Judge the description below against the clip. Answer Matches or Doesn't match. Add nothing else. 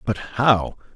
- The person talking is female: Doesn't match